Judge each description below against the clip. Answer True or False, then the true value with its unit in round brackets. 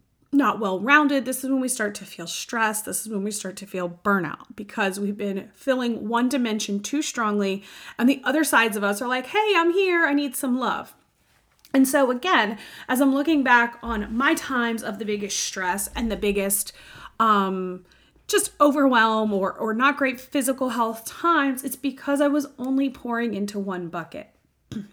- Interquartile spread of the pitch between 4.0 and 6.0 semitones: True (5.2 semitones)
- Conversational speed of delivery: True (190 wpm)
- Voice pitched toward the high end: True (235 Hz)